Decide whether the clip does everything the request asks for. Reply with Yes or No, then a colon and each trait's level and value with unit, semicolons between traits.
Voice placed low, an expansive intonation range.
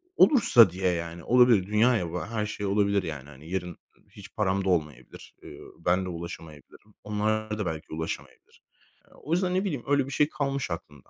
Yes: low, 100 Hz; wide, 6.0 semitones